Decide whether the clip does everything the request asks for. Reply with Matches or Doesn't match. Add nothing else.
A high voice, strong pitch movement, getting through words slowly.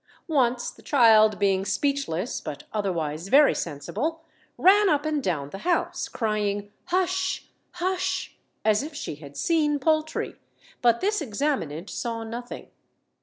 Matches